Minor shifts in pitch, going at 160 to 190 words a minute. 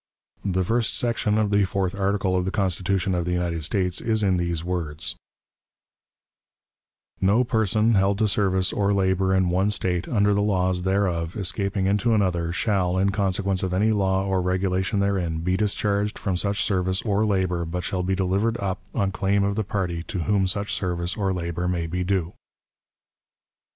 Yes: narrow, 2.0 semitones; average, 175 wpm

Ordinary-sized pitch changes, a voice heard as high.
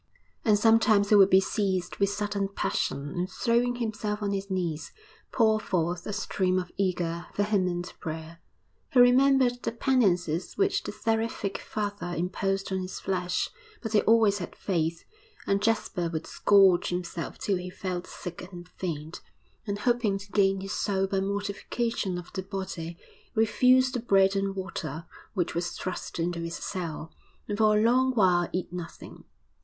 Yes: average, 3.2 semitones; high, 195 Hz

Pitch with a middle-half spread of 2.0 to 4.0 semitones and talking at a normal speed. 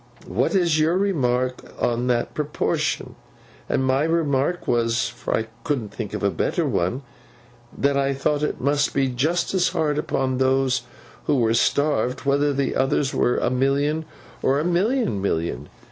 Yes: average, 3.7 semitones; average, 155 wpm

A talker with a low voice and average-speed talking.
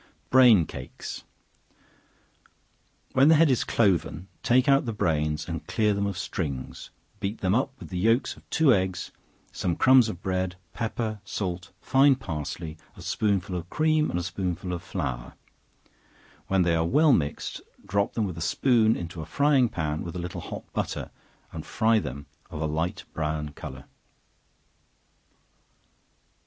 Yes: very low, 95 Hz; average, 155 wpm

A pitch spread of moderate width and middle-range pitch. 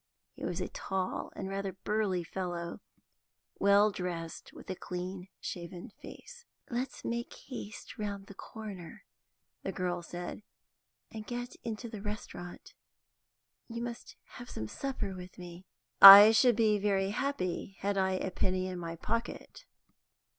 No: average, 3.3 semitones; high, 195 Hz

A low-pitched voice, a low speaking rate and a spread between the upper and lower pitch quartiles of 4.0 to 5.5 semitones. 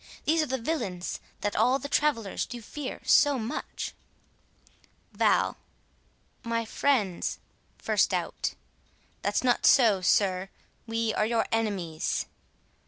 No: high, 230 Hz; slow, 115 wpm; average, 4.5 semitones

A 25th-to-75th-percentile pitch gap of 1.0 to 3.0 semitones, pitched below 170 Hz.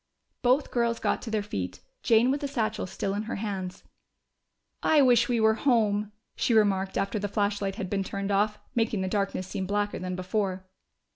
No: narrow, 2.6 semitones; high, 205 Hz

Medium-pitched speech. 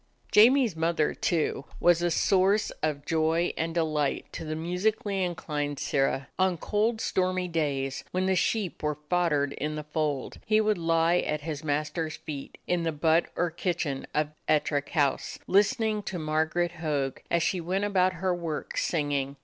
Yes: medium, 165 Hz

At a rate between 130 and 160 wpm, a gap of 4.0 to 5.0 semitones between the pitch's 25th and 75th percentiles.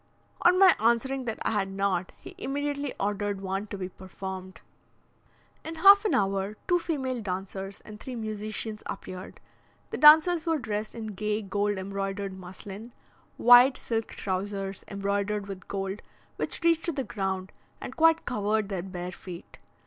Yes: average, 155 wpm; average, 4.6 semitones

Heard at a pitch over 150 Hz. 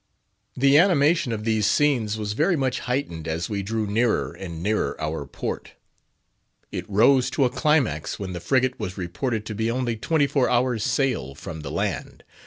No: low, 115 Hz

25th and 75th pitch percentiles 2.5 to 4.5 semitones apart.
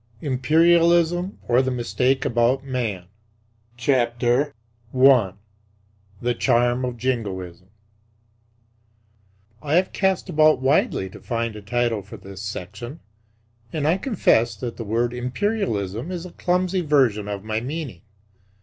No: average, 5.1 semitones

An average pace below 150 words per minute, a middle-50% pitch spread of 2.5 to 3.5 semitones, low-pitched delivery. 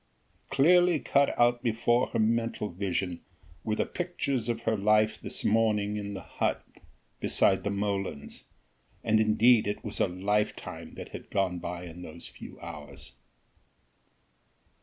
Yes: average, 140 wpm; average, 3.1 semitones; low, 105 Hz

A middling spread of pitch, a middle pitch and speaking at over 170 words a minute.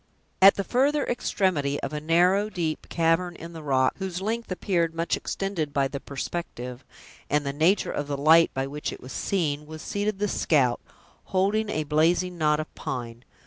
Yes: average, 4.7 semitones; medium, 165 Hz; average, 185 wpm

